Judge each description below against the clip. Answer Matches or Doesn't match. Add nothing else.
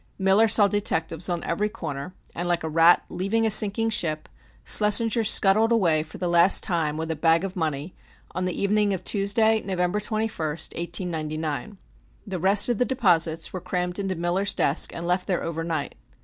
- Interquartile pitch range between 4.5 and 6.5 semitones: Doesn't match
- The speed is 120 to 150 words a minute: Doesn't match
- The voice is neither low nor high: Matches